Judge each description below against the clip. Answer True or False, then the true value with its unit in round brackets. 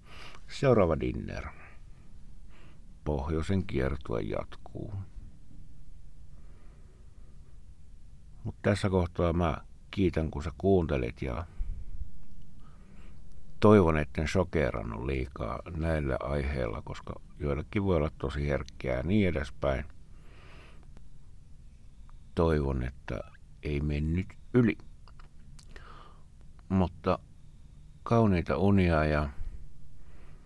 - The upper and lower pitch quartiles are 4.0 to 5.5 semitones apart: False (3.4 semitones)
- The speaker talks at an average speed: False (75 wpm)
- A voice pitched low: True (75 Hz)